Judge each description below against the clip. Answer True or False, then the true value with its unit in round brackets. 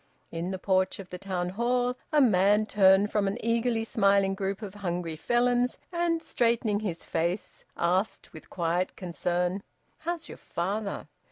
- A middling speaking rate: True (155 wpm)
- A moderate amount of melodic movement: True (4.3 semitones)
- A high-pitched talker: True (200 Hz)